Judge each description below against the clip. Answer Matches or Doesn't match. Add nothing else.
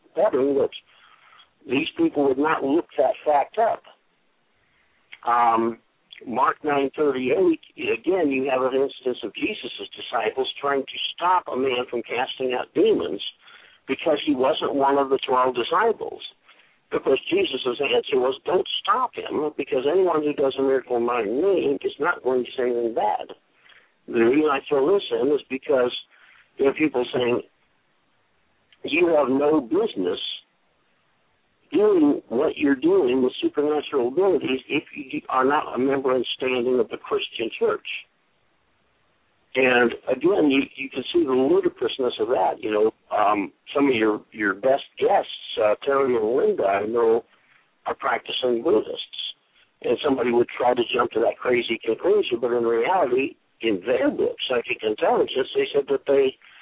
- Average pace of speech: Matches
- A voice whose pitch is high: Matches